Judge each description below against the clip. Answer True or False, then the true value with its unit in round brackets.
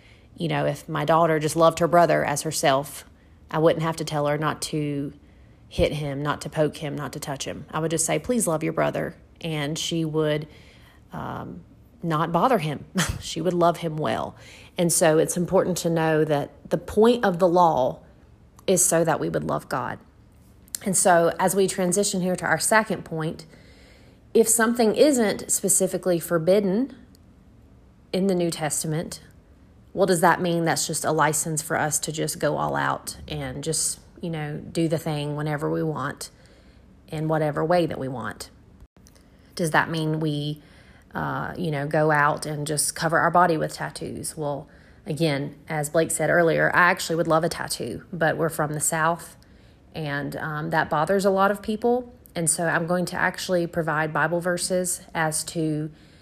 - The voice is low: False (160 Hz)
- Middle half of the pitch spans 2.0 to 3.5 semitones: True (2.8 semitones)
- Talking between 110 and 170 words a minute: False (180 wpm)